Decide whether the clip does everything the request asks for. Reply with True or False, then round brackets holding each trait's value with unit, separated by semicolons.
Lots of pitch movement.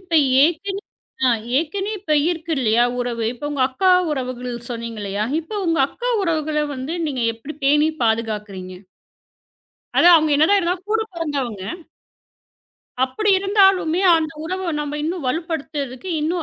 True (5.9 semitones)